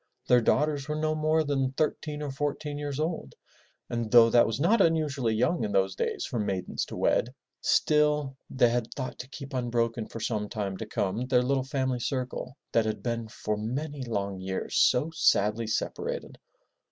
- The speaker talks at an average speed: Yes, average, 180 wpm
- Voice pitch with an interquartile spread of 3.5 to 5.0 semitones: Yes, average, 4.6 semitones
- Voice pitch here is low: Yes, low, 125 Hz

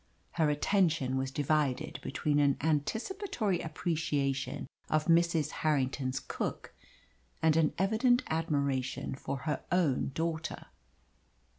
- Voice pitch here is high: No, medium, 155 Hz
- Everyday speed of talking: No, slow, 105 wpm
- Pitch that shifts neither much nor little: Yes, average, 3.3 semitones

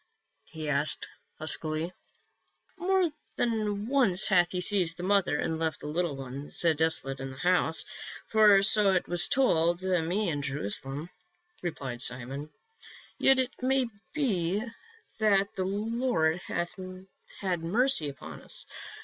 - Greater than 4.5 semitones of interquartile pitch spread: Yes, average, 5.2 semitones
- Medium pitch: Yes, medium, 175 Hz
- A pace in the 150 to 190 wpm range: No, average, 140 wpm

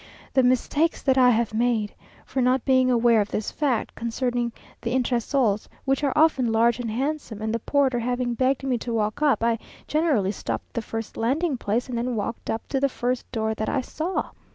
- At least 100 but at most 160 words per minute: No, fast, 205 wpm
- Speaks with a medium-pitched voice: No, high, 245 Hz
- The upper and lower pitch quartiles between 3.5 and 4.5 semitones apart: No, average, 2.8 semitones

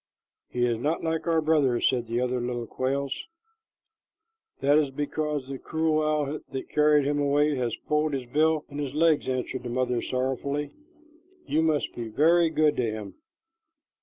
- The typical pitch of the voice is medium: Yes, medium, 145 Hz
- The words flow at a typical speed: Yes, average, 165 wpm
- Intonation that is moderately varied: Yes, average, 3.2 semitones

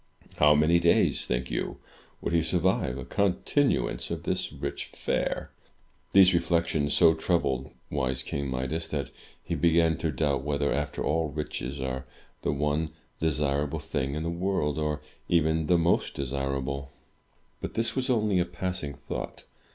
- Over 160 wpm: No, average, 150 wpm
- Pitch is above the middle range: No, very low, 75 Hz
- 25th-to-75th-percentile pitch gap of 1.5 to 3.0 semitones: No, average, 3.4 semitones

